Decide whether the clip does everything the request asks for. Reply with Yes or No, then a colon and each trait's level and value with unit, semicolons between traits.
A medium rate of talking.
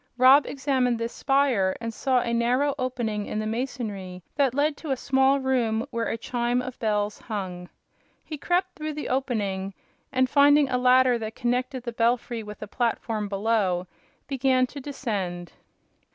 Yes: average, 165 wpm